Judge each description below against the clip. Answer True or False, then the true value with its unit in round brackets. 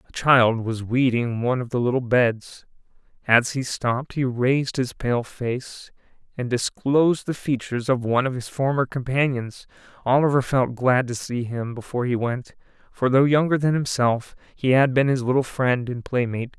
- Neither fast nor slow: True (175 wpm)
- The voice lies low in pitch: True (125 Hz)